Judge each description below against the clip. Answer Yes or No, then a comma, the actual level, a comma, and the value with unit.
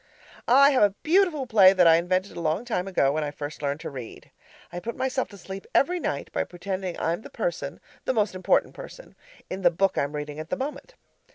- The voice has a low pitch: No, high, 190 Hz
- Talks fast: Yes, fast, 220 wpm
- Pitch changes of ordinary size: No, wide, 7.4 semitones